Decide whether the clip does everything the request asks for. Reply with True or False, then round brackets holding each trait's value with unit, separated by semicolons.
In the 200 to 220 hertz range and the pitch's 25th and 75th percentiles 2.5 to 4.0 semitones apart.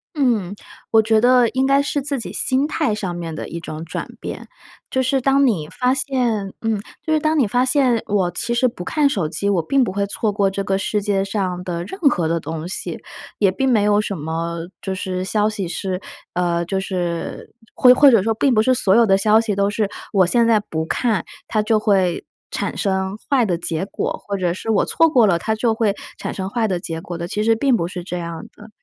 False (205 Hz; 4.7 semitones)